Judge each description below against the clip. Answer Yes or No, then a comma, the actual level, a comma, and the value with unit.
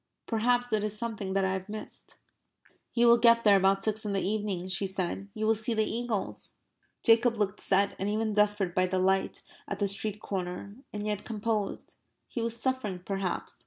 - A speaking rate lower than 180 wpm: No, average, 195 wpm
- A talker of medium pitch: No, high, 210 Hz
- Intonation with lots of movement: No, narrow, 2.4 semitones